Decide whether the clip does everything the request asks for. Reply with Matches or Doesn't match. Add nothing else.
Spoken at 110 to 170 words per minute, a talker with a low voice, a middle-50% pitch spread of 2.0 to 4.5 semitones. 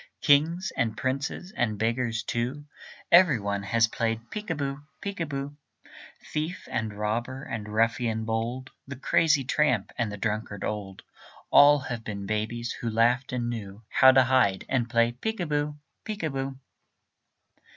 Matches